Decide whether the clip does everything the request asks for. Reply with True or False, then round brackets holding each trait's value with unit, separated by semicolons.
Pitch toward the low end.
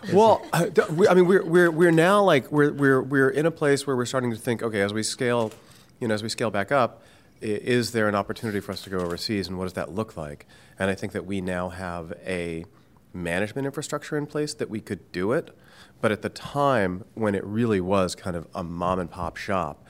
True (110 Hz)